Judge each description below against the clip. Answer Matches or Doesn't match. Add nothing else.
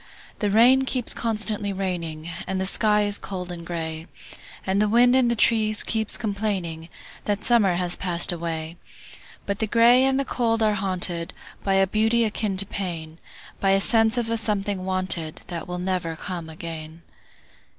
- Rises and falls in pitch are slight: Doesn't match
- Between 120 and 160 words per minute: Matches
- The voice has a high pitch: Matches